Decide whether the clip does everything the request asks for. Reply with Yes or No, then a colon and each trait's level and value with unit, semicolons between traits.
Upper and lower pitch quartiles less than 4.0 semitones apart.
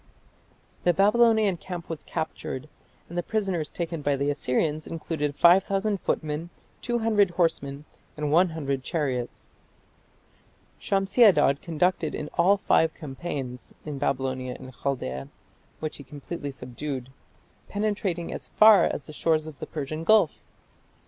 No: average, 4.7 semitones